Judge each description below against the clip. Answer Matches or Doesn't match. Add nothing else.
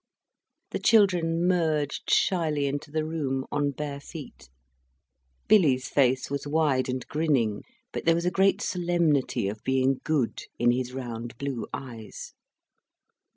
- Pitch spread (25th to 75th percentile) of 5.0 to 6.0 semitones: Doesn't match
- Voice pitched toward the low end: Doesn't match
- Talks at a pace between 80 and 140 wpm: Matches